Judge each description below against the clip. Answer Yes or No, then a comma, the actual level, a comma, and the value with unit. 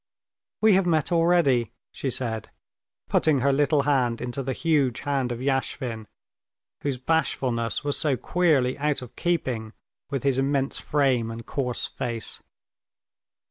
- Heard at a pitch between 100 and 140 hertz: Yes, low, 135 Hz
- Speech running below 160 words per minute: Yes, average, 140 wpm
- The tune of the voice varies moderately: Yes, average, 3.1 semitones